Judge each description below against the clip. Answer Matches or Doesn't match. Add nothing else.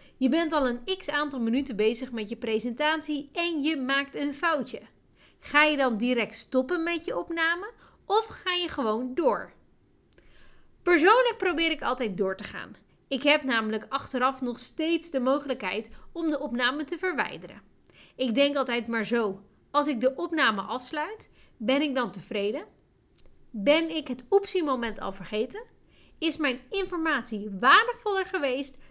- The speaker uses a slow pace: Doesn't match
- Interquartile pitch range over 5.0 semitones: Matches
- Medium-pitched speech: Doesn't match